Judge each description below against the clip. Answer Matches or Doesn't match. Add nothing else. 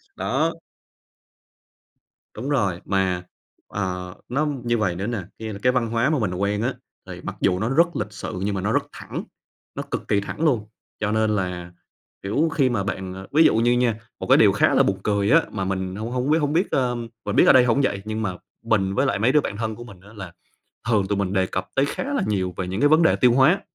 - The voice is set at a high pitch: Doesn't match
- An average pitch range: Matches